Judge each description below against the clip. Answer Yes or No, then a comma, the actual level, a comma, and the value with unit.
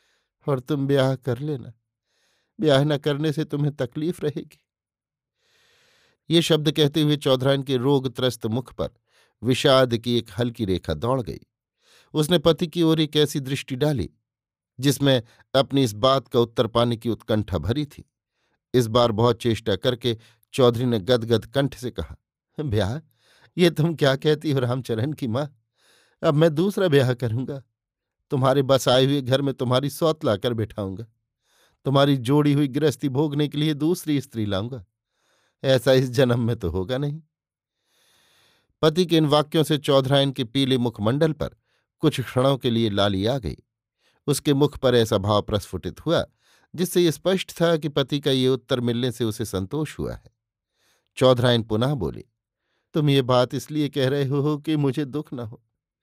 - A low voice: Yes, low, 130 Hz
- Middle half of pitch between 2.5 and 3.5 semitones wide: No, average, 4.0 semitones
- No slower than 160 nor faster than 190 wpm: Yes, average, 165 wpm